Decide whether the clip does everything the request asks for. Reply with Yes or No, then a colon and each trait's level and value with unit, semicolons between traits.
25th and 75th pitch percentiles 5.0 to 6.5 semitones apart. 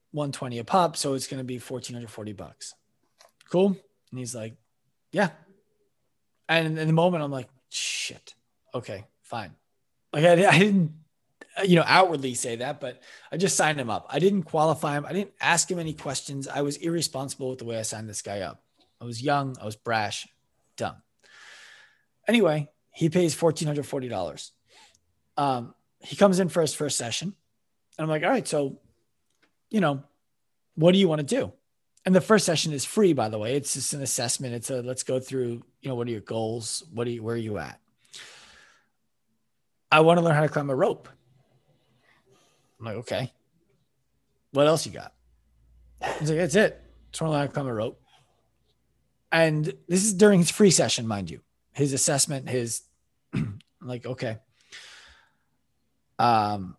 Yes: wide, 5.4 semitones